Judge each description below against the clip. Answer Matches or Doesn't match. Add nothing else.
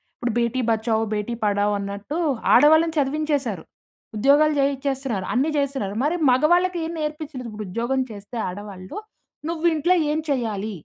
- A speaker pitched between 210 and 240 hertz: Doesn't match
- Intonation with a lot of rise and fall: Matches